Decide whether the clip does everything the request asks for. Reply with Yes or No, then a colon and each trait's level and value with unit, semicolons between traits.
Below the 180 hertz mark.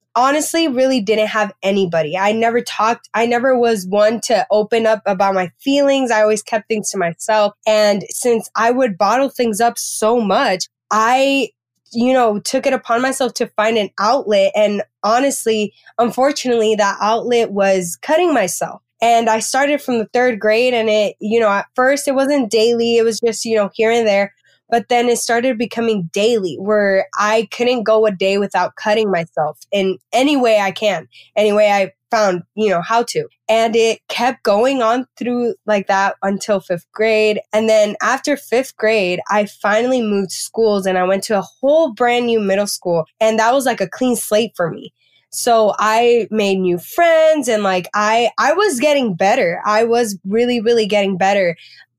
No: high, 220 Hz